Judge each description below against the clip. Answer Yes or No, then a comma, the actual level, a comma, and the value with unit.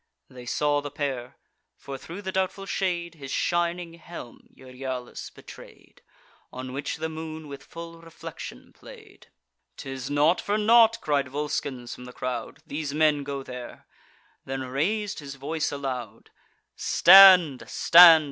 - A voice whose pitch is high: No, medium, 145 Hz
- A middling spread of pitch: Yes, average, 4.2 semitones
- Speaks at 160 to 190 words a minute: No, average, 140 wpm